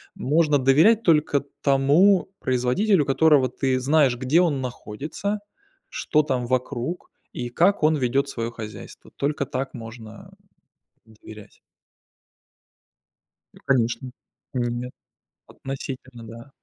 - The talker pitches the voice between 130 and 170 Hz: Yes, low, 135 Hz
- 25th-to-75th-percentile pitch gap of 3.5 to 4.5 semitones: Yes, average, 3.8 semitones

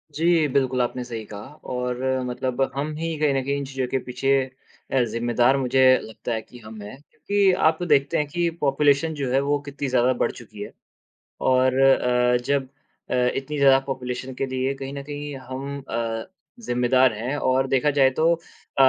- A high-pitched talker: No, low, 135 Hz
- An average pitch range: No, narrow, 2.3 semitones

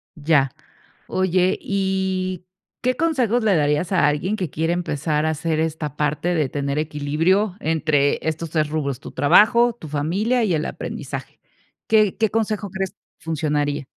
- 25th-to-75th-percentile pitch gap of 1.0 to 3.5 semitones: No, average, 4.4 semitones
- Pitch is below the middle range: No, medium, 165 Hz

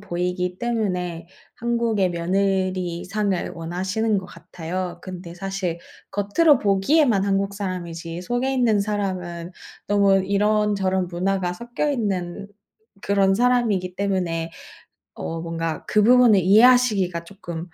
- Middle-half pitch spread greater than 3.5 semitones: No, average, 2.9 semitones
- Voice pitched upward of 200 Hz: No, high, 195 Hz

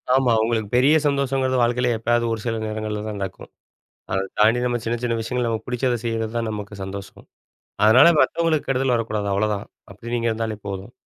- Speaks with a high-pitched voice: No, low, 115 Hz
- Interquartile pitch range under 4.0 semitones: Yes, narrow, 2.5 semitones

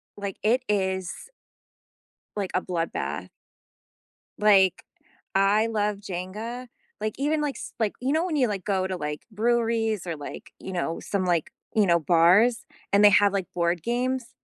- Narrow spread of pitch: No, average, 4.0 semitones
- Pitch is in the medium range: No, high, 205 Hz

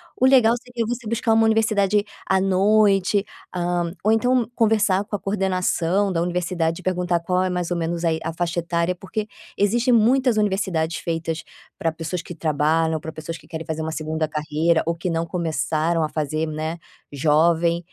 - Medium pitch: Yes, medium, 175 Hz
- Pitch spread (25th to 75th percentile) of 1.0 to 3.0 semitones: No, average, 3.9 semitones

